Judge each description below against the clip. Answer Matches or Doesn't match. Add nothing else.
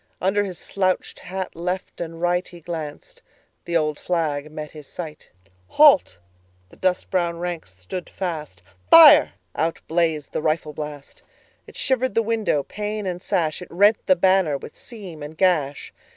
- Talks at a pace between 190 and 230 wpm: Doesn't match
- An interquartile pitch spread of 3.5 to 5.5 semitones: Matches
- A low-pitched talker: Doesn't match